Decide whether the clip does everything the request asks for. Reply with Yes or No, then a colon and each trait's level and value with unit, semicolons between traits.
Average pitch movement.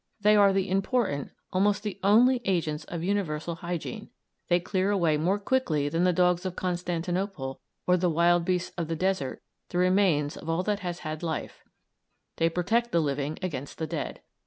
Yes: average, 3.2 semitones